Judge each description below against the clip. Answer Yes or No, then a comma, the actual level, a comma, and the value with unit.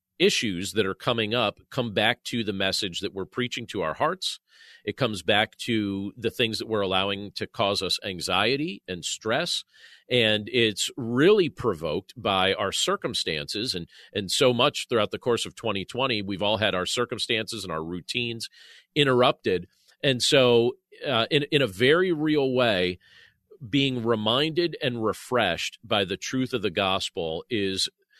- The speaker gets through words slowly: No, average, 160 wpm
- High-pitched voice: No, low, 115 Hz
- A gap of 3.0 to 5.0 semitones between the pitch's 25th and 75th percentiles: Yes, average, 4.2 semitones